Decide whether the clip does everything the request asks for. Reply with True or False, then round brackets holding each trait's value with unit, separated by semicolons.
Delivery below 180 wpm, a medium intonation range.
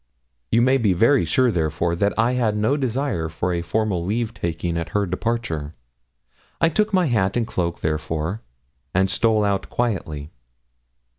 False (160 wpm; 5.7 semitones)